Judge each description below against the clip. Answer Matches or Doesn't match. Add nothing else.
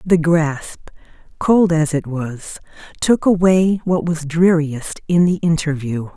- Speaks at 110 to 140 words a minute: Matches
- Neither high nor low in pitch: Matches